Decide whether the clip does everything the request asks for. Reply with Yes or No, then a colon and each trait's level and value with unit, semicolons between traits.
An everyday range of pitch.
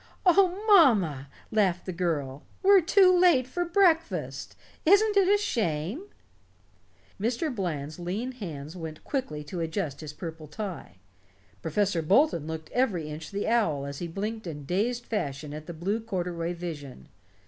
No: wide, 8.4 semitones